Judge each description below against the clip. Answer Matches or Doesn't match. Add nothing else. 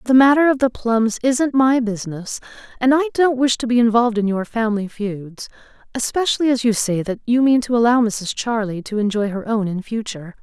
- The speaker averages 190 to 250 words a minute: Matches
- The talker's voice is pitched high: Matches